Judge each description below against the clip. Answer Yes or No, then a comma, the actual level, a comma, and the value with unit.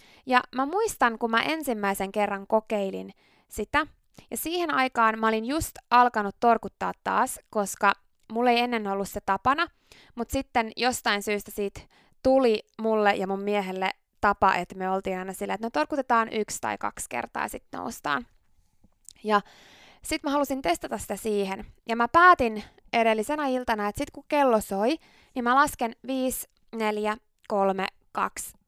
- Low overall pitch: No, high, 220 Hz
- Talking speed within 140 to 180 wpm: Yes, fast, 155 wpm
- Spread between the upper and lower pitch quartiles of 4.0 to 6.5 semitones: Yes, average, 4.3 semitones